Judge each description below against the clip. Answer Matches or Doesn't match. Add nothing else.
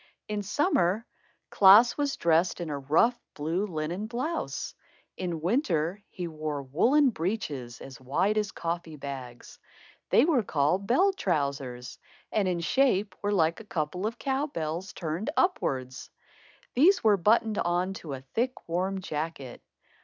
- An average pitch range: Doesn't match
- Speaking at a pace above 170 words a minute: Doesn't match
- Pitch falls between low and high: Matches